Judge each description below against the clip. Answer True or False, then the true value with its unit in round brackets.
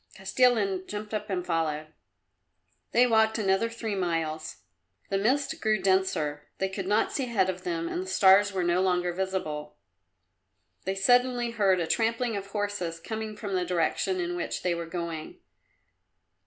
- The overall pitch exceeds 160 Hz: True (190 Hz)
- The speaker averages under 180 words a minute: True (160 wpm)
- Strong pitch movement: False (3.6 semitones)